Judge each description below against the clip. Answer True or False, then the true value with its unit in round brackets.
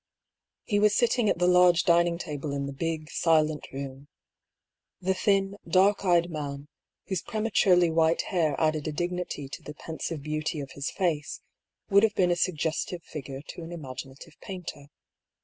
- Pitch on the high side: False (165 Hz)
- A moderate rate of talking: True (165 wpm)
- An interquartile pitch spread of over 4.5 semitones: False (3.3 semitones)